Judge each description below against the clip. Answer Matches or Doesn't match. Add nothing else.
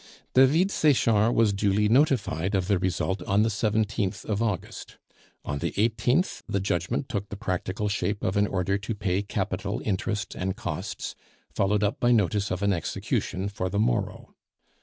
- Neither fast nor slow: Matches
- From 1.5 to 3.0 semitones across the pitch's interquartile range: Matches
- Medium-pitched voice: Doesn't match